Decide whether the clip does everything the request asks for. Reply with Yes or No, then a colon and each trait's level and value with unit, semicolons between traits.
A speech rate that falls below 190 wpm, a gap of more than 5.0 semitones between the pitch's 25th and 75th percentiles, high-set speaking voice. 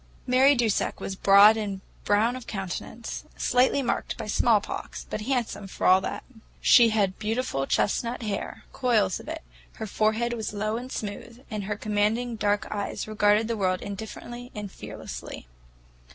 No: average, 155 wpm; average, 2.8 semitones; high, 215 Hz